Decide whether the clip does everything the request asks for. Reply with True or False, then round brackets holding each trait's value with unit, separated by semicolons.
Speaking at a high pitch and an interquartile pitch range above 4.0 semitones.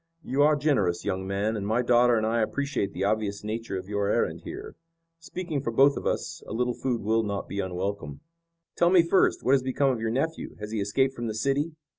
False (115 Hz; 5.2 semitones)